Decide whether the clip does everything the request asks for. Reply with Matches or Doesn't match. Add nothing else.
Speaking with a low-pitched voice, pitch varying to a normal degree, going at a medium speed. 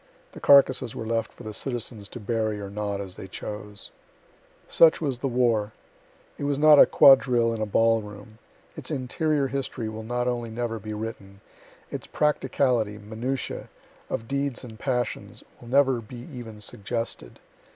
Matches